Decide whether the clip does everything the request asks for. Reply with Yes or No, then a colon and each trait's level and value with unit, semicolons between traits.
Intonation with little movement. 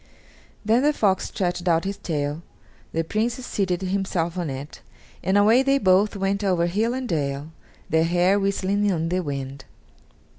No: average, 3.7 semitones